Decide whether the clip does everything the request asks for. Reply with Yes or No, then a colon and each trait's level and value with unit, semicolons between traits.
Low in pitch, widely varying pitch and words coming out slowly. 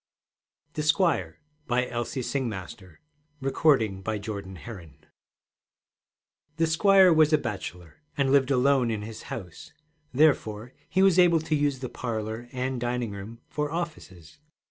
Yes: low, 125 Hz; wide, 5.9 semitones; slow, 120 wpm